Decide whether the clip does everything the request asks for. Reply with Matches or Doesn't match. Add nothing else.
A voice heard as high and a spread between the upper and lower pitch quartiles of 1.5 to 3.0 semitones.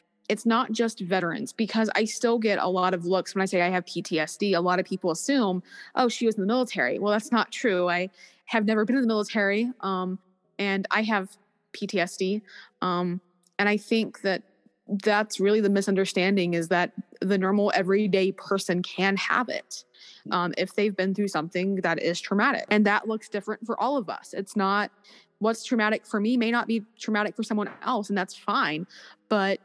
Matches